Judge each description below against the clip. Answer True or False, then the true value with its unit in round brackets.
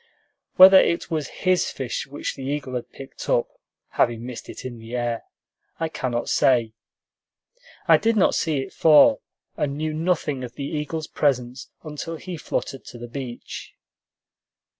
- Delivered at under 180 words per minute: True (160 wpm)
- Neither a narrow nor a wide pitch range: True (4.3 semitones)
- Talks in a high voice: False (140 Hz)